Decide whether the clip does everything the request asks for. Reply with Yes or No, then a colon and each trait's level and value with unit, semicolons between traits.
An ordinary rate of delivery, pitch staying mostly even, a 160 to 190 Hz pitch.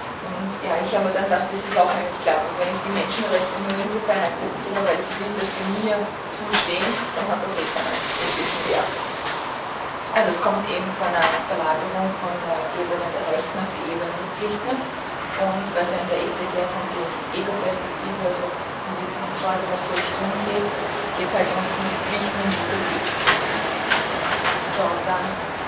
No: fast, 175 wpm; narrow, 2.1 semitones; medium, 185 Hz